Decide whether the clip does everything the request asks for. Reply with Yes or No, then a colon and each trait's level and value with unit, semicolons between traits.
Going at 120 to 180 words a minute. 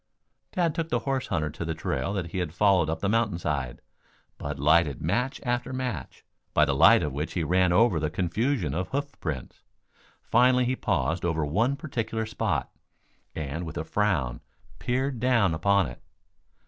Yes: average, 175 wpm